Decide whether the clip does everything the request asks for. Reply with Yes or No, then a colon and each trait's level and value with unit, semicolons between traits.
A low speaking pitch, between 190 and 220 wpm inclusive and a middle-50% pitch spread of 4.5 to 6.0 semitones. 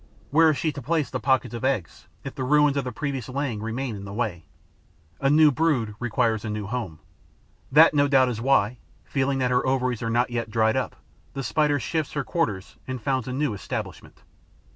No: low, 130 Hz; fast, 205 wpm; average, 3.9 semitones